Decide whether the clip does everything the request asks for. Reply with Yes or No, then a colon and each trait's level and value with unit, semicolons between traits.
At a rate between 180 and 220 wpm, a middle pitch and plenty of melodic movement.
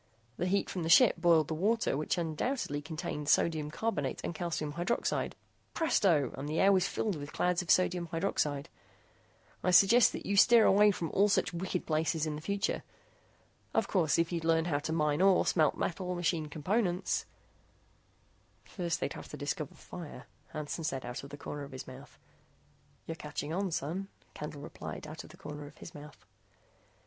No: average, 185 wpm; medium, 165 Hz; average, 3.6 semitones